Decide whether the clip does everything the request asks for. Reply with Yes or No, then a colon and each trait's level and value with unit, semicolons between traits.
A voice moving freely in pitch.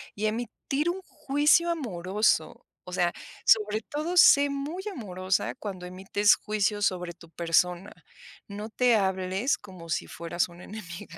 Yes: wide, 5.7 semitones